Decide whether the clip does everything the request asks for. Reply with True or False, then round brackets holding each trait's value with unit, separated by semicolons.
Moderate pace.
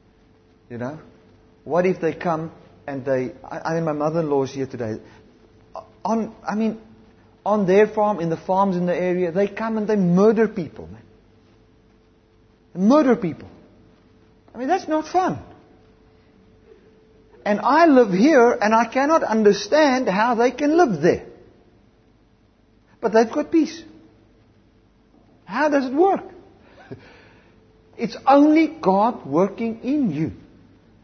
False (130 wpm)